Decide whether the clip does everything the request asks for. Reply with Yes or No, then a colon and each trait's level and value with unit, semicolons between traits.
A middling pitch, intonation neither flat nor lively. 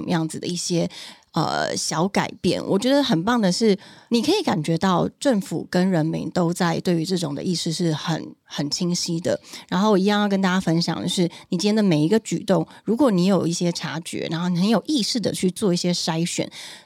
Yes: medium, 175 Hz; average, 3.0 semitones